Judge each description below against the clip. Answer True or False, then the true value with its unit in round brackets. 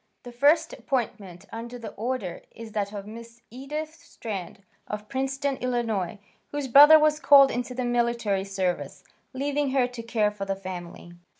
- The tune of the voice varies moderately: True (4.6 semitones)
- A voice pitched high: True (235 Hz)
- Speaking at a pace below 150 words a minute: False (160 wpm)